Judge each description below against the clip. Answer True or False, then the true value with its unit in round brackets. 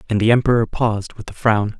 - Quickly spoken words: True (235 wpm)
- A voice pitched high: False (110 Hz)